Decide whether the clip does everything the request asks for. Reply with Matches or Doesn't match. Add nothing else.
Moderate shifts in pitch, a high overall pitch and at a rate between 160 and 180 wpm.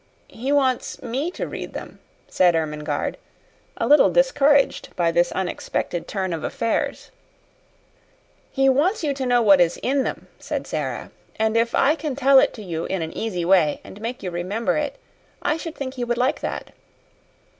Doesn't match